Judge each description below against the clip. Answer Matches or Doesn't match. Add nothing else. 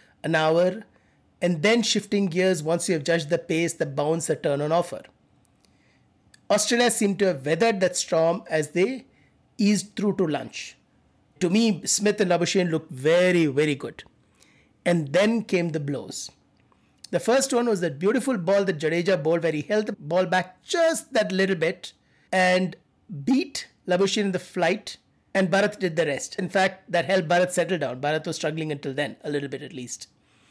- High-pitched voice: Doesn't match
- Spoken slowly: Doesn't match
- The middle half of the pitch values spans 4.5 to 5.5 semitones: Doesn't match